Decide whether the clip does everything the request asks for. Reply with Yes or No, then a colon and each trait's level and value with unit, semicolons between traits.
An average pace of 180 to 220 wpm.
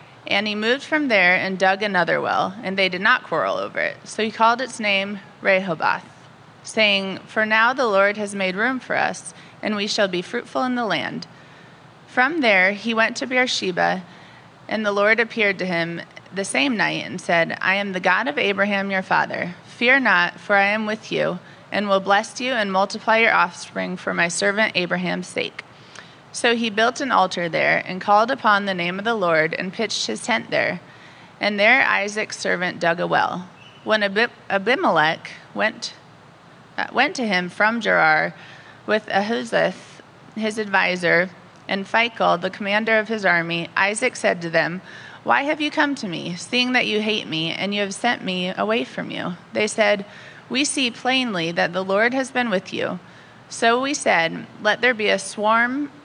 Yes: average, 185 wpm